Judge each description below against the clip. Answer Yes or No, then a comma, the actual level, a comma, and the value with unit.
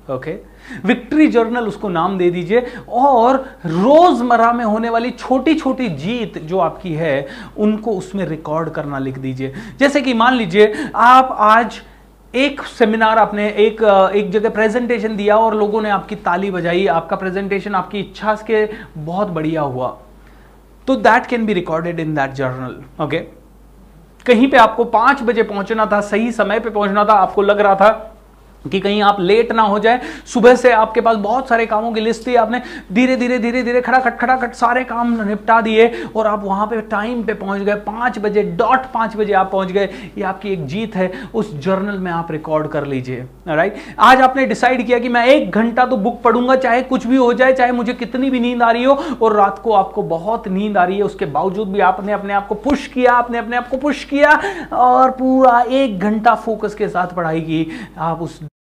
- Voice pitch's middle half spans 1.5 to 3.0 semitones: No, average, 4.0 semitones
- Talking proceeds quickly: Yes, fast, 200 wpm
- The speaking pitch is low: No, high, 215 Hz